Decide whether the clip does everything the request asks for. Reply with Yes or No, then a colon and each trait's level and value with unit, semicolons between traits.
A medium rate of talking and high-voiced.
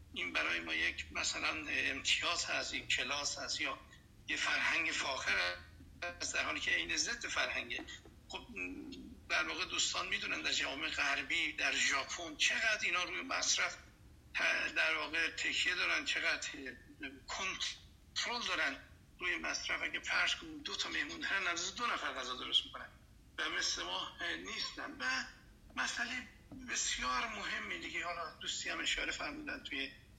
Yes: average, 140 wpm; high, 240 Hz